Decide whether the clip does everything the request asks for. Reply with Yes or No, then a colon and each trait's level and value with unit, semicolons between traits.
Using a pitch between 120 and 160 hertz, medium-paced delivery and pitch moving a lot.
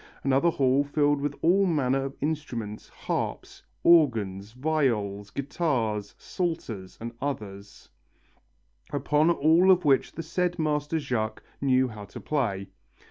No: medium, 140 Hz; slow, 125 wpm; wide, 6.2 semitones